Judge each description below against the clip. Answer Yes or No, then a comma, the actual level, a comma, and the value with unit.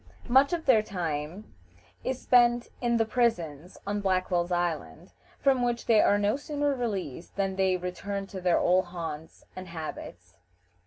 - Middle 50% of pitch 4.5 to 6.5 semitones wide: Yes, wide, 5.4 semitones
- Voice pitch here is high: Yes, high, 195 Hz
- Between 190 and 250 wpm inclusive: No, average, 155 wpm